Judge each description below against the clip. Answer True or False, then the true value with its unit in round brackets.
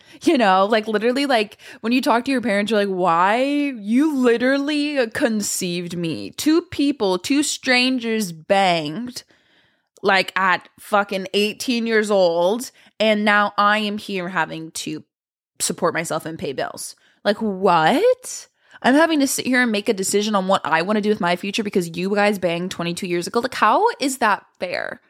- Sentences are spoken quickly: False (175 wpm)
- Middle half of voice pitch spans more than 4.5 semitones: True (4.9 semitones)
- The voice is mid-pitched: False (210 Hz)